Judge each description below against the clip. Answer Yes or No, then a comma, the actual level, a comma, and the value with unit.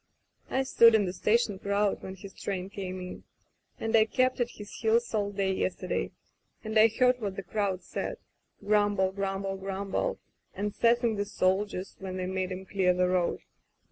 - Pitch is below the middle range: No, high, 200 Hz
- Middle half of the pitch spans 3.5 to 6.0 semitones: No, narrow, 2.5 semitones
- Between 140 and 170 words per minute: No, average, 180 wpm